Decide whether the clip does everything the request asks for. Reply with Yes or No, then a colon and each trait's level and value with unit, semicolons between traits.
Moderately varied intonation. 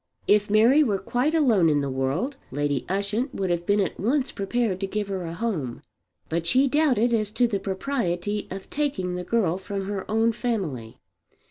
Yes: average, 4.9 semitones